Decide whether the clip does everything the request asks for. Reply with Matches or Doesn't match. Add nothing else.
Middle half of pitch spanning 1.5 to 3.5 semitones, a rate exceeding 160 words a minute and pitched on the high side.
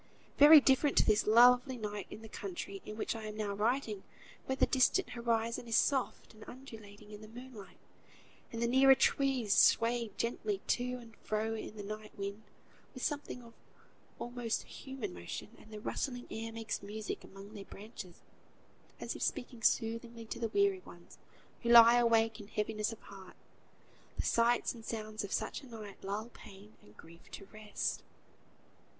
Matches